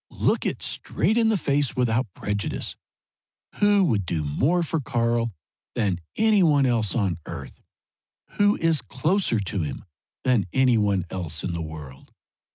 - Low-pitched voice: Yes, low, 120 Hz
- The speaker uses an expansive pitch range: Yes, wide, 8.7 semitones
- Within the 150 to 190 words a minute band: Yes, average, 155 wpm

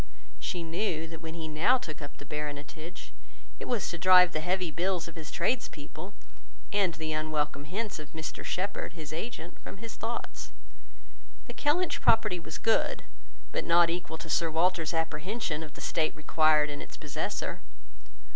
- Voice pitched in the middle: Yes, medium, 165 Hz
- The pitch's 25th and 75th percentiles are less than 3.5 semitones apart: Yes, average, 3.1 semitones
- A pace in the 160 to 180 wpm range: Yes, average, 165 wpm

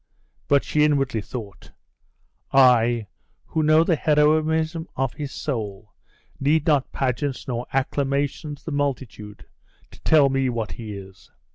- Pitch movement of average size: Yes, average, 4.2 semitones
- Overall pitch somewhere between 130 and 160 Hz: Yes, low, 135 Hz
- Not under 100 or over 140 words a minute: Yes, slow, 135 wpm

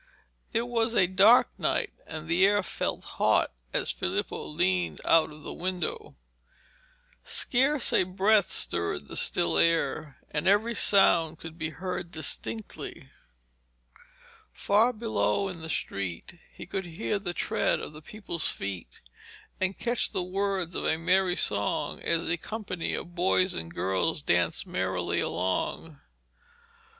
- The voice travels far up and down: No, average, 4.5 semitones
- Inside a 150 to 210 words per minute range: No, average, 140 wpm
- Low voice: No, medium, 175 Hz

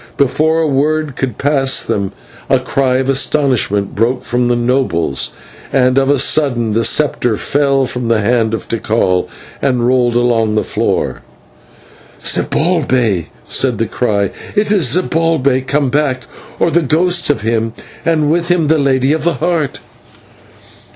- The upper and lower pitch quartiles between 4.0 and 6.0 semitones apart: Yes, average, 4.3 semitones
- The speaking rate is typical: Yes, average, 150 wpm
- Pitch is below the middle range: Yes, low, 130 Hz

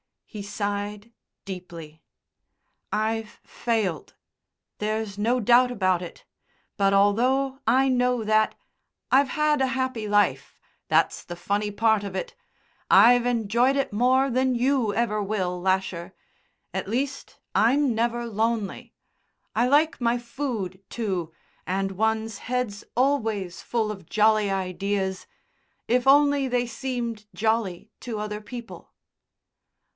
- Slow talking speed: Yes, slow, 120 wpm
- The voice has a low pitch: No, high, 220 Hz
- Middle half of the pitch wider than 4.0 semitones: No, average, 3.7 semitones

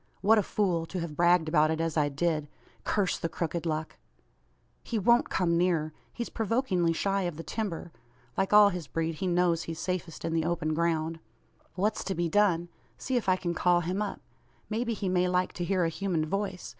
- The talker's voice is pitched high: No, medium, 175 Hz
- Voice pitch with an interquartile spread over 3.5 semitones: No, average, 2.9 semitones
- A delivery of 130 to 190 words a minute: No, fast, 205 wpm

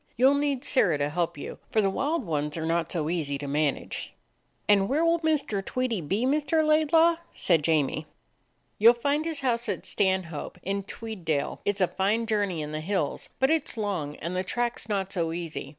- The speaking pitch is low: No, high, 195 Hz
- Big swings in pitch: Yes, wide, 7.8 semitones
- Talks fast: Yes, fast, 215 wpm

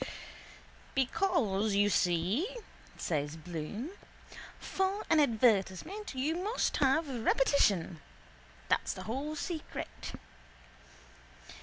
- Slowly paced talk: Yes, slow, 85 wpm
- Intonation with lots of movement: Yes, wide, 8.9 semitones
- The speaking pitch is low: No, very high, 255 Hz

